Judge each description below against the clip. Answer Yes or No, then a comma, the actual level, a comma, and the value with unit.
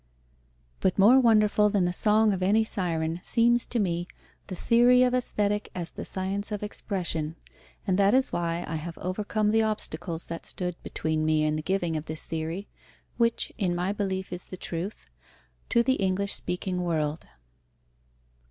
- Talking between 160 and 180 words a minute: Yes, average, 170 wpm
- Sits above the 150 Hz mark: Yes, high, 190 Hz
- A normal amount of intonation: Yes, average, 3.9 semitones